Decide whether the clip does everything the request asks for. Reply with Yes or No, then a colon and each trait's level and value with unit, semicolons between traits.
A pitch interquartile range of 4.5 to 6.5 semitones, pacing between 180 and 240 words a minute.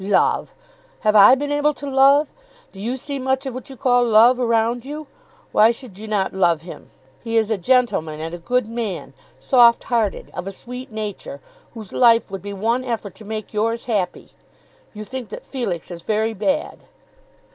No: average, 3.8 semitones; average, 190 wpm